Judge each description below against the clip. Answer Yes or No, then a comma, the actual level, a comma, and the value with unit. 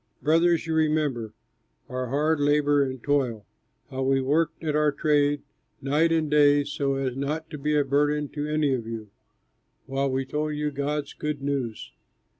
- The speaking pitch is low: No, medium, 145 Hz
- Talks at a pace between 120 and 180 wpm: Yes, average, 170 wpm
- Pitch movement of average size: No, narrow, 1.9 semitones